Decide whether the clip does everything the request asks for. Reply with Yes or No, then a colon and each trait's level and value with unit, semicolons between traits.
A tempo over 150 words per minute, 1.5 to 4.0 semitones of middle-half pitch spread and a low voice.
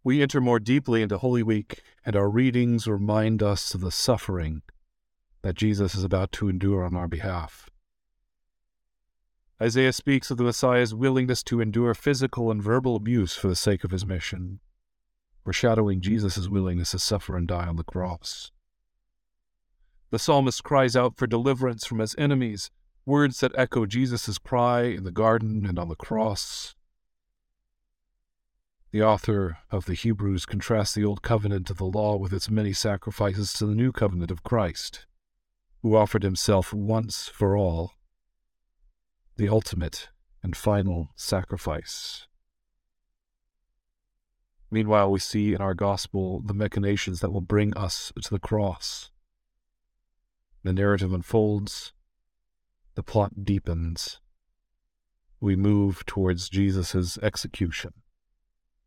No: slow, 135 wpm; average, 3.4 semitones; low, 105 Hz